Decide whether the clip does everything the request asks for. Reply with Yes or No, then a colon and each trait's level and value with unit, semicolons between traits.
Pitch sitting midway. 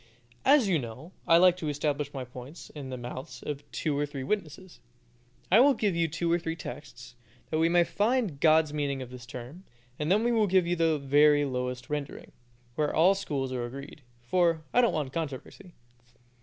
Yes: medium, 150 Hz